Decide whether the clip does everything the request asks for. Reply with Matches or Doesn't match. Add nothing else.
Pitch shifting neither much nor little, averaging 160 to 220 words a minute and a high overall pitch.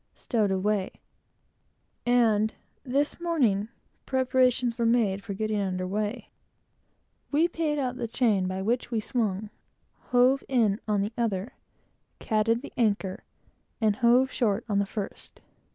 Doesn't match